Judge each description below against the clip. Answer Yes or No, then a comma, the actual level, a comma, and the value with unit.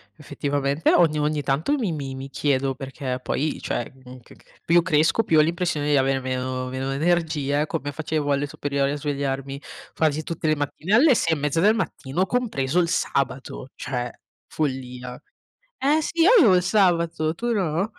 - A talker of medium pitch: Yes, medium, 150 Hz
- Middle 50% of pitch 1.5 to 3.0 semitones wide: No, average, 3.8 semitones